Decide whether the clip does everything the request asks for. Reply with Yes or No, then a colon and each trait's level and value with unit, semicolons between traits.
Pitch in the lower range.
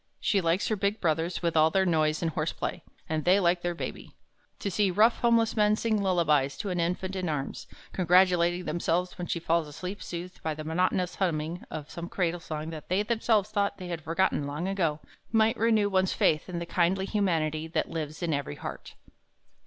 No: medium, 175 Hz